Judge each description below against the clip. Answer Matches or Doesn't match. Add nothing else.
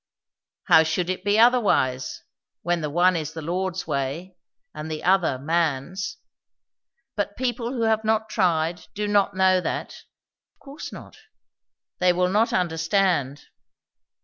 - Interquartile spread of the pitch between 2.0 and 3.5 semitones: Doesn't match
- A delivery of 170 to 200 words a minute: Doesn't match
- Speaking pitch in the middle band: Matches